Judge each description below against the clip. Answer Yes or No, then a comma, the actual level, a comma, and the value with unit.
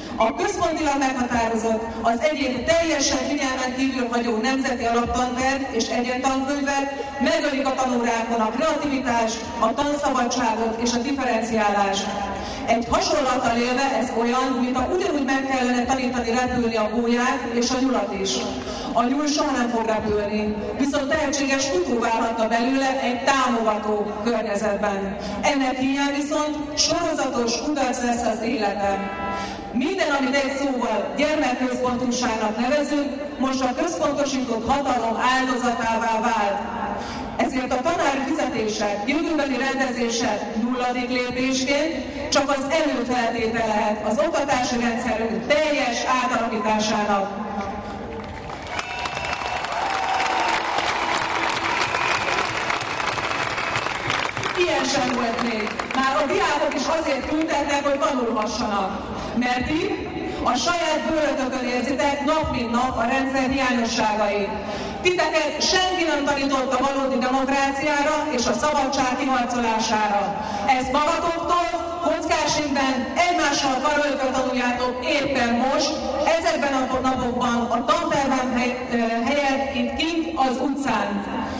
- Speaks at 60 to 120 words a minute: Yes, slow, 105 wpm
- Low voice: No, very high, 255 Hz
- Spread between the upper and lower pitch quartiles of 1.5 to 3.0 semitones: No, average, 3.6 semitones